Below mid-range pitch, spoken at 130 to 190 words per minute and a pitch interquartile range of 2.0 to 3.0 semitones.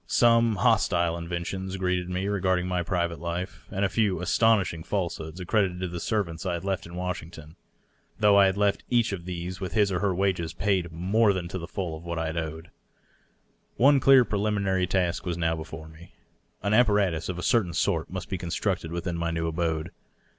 No: very low, 90 Hz; average, 200 wpm; average, 2.7 semitones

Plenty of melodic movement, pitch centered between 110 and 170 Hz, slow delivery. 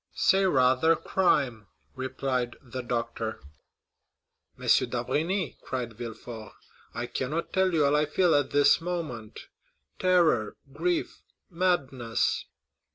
Yes: wide, 5.9 semitones; low, 135 Hz; slow, 100 wpm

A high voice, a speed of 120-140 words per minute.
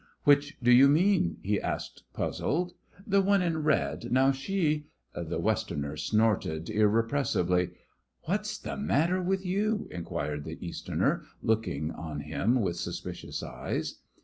No: low, 130 Hz; slow, 135 wpm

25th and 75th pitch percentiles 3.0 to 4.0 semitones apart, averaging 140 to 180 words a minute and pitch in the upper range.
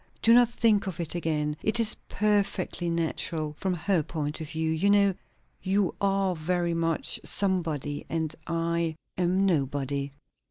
No: average, 3.7 semitones; average, 150 wpm; medium, 170 Hz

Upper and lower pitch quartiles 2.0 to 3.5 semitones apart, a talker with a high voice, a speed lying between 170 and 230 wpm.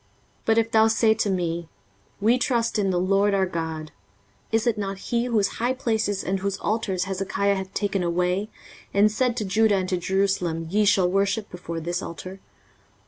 Yes: average, 3.1 semitones; high, 195 Hz; average, 190 wpm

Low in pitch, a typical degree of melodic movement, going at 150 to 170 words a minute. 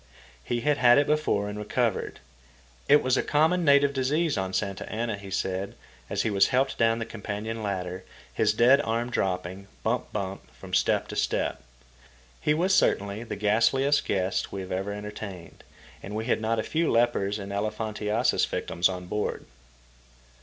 Yes: low, 110 Hz; average, 4.4 semitones; average, 165 wpm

